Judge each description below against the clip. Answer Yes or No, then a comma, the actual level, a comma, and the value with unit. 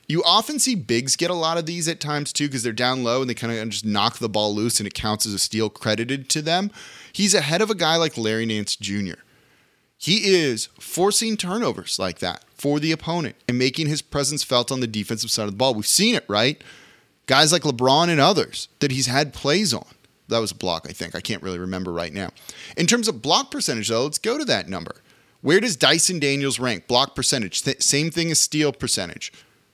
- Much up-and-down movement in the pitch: Yes, wide, 7.1 semitones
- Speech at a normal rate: No, fast, 230 wpm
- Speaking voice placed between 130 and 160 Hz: Yes, low, 135 Hz